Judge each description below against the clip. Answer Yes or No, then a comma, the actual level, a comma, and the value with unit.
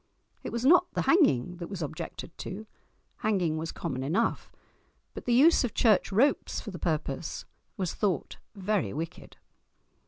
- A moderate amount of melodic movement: No, wide, 6.1 semitones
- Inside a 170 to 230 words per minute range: No, average, 150 wpm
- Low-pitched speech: No, high, 190 Hz